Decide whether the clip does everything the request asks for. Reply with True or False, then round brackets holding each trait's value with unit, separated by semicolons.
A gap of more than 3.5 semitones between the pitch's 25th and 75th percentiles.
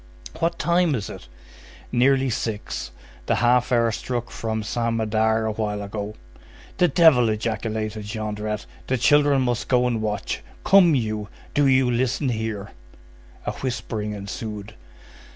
False (3.2 semitones)